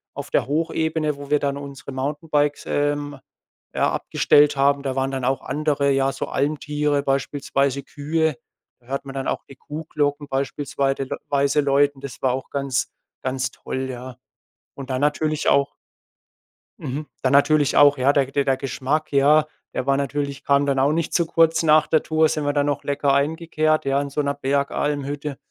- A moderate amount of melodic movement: No, narrow, 1.5 semitones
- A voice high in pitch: No, medium, 140 Hz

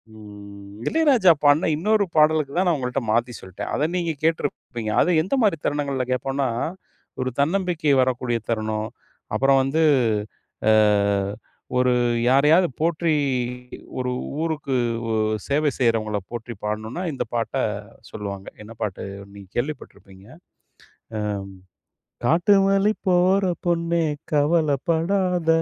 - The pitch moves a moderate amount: No, wide, 6.5 semitones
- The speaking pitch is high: No, medium, 145 Hz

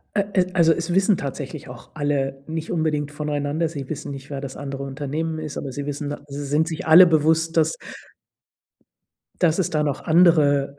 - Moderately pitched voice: Yes, medium, 150 Hz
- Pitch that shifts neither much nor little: No, narrow, 2.3 semitones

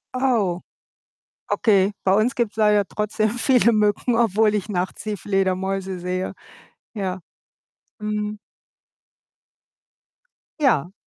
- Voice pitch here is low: No, high, 210 Hz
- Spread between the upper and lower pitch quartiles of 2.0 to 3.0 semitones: Yes, narrow, 2.5 semitones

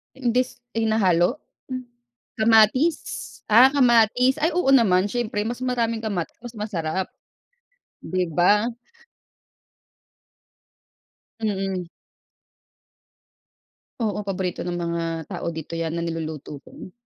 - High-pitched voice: Yes, high, 210 Hz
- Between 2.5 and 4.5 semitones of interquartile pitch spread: No, average, 5.3 semitones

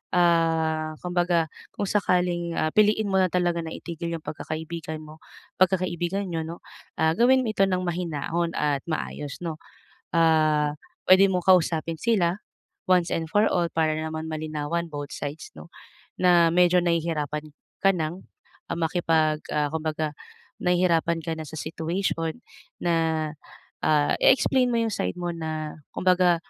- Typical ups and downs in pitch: No, narrow, 2.3 semitones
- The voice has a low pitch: No, medium, 165 Hz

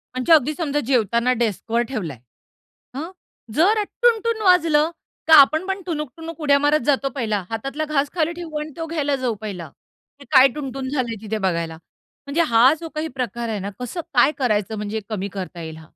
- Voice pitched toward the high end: Yes, very high, 275 Hz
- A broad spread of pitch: Yes, wide, 5.9 semitones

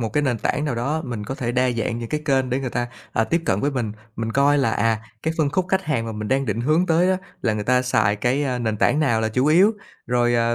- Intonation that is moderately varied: Yes, average, 4.2 semitones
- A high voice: No, low, 125 Hz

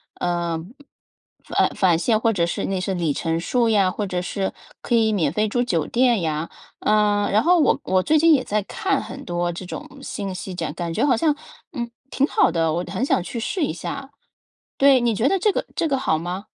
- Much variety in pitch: Yes, wide, 6.1 semitones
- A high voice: Yes, high, 205 Hz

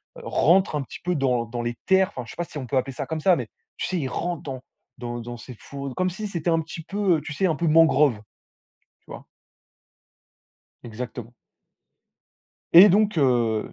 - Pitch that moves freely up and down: Yes, wide, 6.2 semitones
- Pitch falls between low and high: Yes, medium, 150 Hz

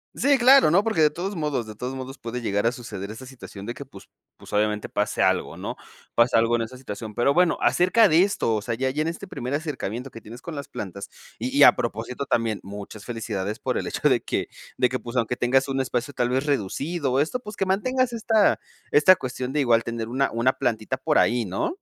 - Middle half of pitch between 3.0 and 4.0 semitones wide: No, average, 5.1 semitones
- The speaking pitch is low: Yes, low, 130 Hz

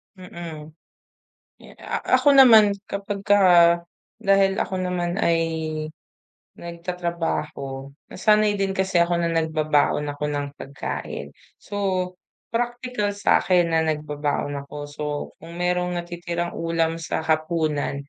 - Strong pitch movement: No, average, 3.6 semitones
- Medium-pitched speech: Yes, medium, 170 Hz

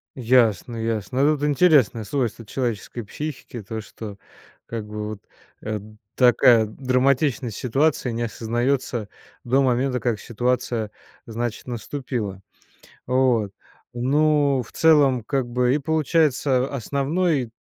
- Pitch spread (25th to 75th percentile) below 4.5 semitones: Yes, average, 3.4 semitones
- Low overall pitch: Yes, low, 125 Hz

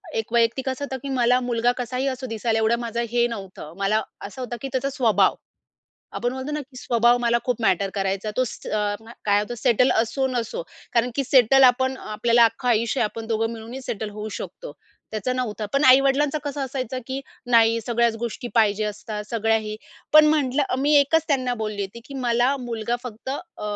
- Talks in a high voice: Yes, high, 240 Hz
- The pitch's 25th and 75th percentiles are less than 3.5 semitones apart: Yes, average, 3.0 semitones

